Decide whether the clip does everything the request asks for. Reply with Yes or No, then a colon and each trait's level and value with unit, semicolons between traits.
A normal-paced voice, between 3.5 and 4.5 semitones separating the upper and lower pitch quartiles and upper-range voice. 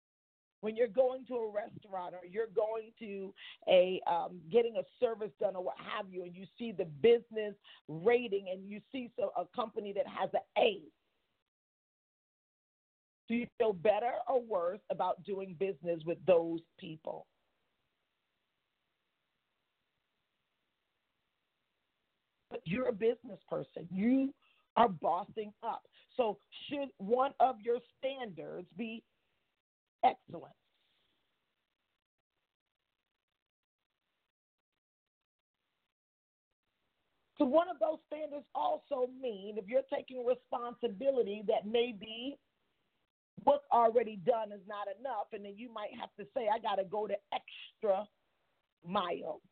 No: slow, 120 wpm; average, 4.2 semitones; high, 225 Hz